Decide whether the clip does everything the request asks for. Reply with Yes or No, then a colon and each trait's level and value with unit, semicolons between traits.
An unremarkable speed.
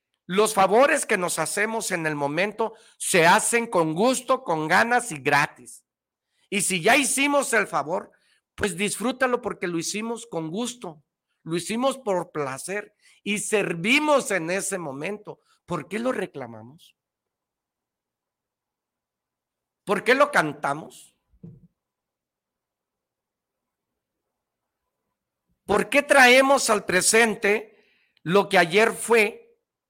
No: slow, 110 wpm